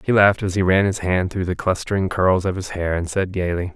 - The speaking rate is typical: No, fast, 270 wpm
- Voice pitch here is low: Yes, very low, 90 Hz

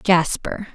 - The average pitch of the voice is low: No, medium, 185 Hz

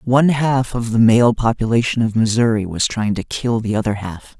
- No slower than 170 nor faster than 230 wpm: Yes, fast, 205 wpm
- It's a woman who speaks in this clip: No, male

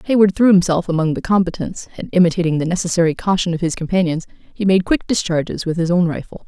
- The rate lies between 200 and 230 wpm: Yes, fast, 205 wpm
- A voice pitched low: No, medium, 175 Hz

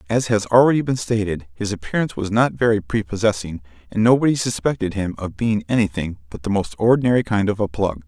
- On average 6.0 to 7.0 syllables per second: Yes, 6.1 syllables/s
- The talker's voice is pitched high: No, low, 105 Hz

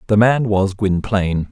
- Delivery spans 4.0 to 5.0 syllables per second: Yes, 4.6 syllables/s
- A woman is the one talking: No, male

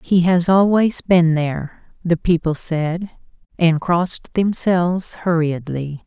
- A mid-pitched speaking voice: Yes, medium, 170 Hz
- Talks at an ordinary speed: No, slow, 120 wpm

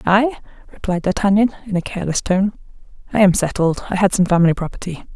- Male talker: No, female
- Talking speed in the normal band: Yes, average, 165 wpm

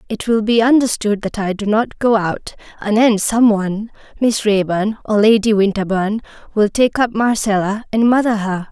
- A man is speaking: No, female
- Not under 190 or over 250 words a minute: No, average, 160 wpm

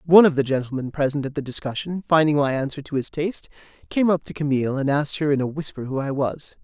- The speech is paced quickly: Yes, fast, 245 wpm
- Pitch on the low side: No, medium, 145 Hz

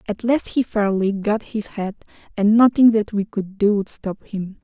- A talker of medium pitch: No, high, 210 Hz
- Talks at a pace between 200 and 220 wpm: Yes, fast, 205 wpm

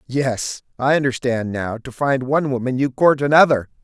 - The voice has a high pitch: No, low, 130 Hz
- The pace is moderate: Yes, average, 170 wpm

